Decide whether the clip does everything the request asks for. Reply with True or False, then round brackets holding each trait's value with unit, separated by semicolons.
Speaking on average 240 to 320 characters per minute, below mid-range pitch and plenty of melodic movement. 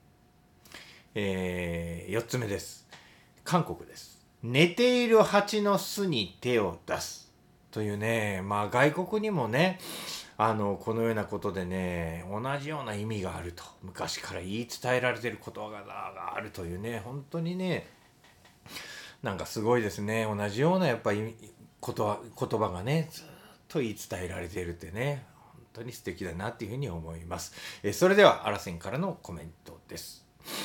True (300 characters per minute; 115 Hz; 6.6 semitones)